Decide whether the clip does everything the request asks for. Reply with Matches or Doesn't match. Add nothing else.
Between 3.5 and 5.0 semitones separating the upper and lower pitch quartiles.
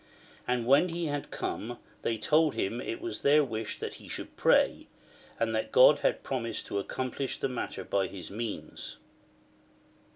Matches